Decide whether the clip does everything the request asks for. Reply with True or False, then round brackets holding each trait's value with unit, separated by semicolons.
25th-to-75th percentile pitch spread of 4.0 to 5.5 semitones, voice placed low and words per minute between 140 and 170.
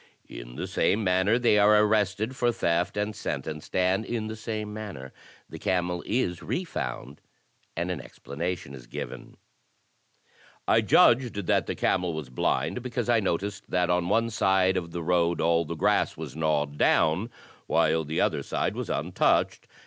True (4.5 semitones; 90 Hz; 165 wpm)